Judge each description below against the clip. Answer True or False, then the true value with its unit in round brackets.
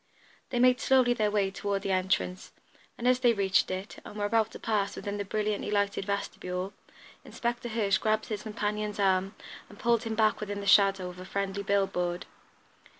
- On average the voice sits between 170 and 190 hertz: False (205 Hz)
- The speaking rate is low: False (190 wpm)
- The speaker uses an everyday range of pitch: False (1.9 semitones)